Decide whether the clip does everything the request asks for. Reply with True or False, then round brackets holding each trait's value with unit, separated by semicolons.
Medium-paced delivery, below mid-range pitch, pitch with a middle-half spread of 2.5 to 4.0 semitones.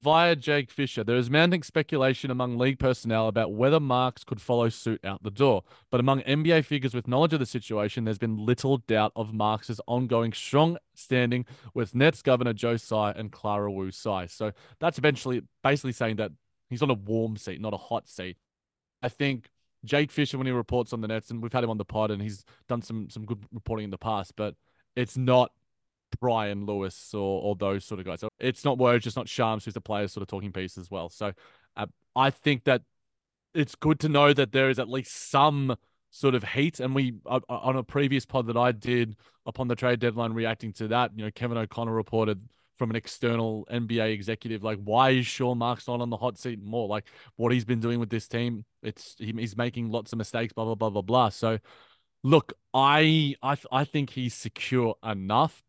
False (215 wpm; 120 Hz; 2.9 semitones)